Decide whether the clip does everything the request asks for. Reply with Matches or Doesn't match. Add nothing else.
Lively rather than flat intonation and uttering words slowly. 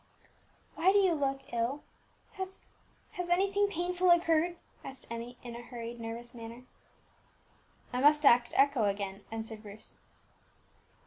Matches